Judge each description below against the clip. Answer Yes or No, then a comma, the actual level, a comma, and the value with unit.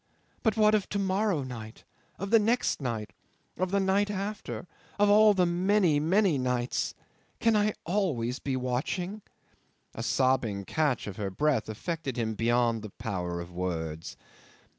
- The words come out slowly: No, average, 155 wpm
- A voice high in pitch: No, medium, 145 Hz